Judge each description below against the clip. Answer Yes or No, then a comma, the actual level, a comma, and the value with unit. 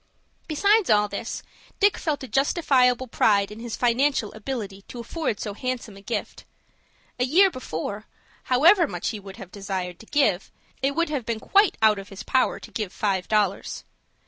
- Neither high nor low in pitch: No, high, 235 Hz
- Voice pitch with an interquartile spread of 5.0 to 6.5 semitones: Yes, wide, 5.5 semitones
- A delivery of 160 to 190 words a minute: Yes, average, 175 wpm